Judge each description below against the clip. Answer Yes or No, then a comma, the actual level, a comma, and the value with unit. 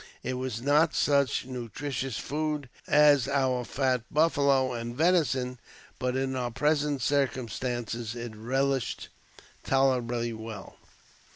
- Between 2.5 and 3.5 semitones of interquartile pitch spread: Yes, average, 2.8 semitones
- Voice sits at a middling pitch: No, low, 130 Hz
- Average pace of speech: No, slow, 110 wpm